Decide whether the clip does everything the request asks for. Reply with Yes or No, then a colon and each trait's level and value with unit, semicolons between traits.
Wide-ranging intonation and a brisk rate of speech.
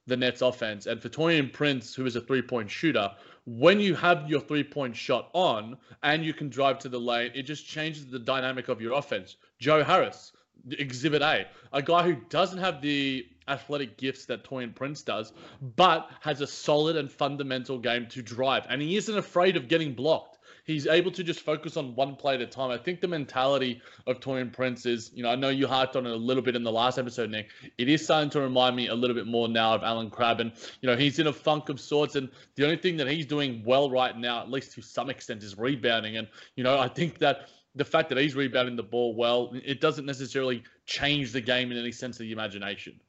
No: average, 3.4 semitones; fast, 235 wpm